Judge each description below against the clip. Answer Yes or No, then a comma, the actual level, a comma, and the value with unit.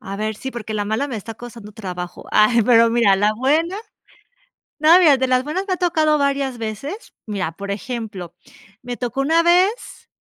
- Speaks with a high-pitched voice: Yes, high, 240 Hz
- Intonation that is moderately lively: No, wide, 5.7 semitones